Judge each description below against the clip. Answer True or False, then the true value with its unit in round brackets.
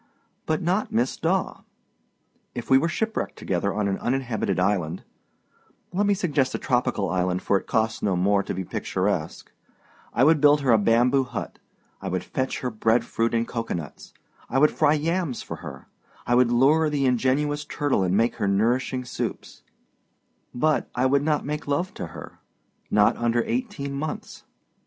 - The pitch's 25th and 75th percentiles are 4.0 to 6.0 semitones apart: True (5.5 semitones)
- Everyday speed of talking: True (170 wpm)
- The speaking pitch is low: True (125 Hz)